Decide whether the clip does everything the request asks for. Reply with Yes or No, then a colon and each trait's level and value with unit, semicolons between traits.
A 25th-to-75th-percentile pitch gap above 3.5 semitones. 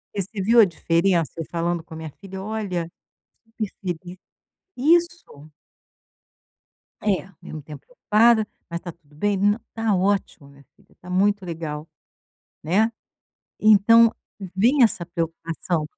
Yes: average, 4.3 semitones